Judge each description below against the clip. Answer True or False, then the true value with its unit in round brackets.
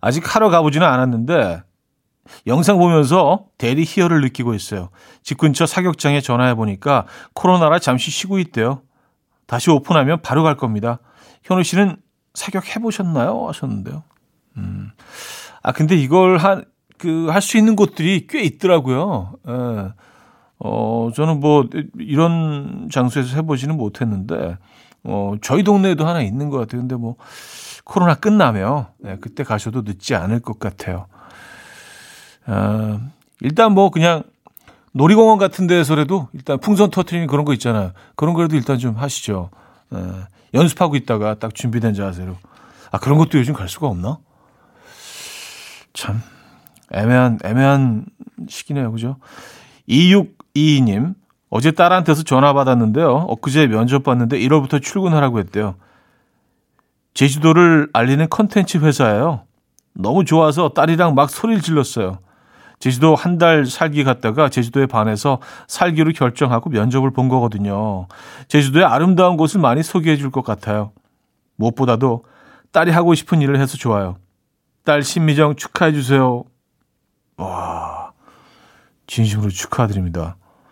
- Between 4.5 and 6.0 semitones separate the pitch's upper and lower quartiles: False (6.6 semitones)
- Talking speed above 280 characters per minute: True (290 characters per minute)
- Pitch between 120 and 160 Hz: True (140 Hz)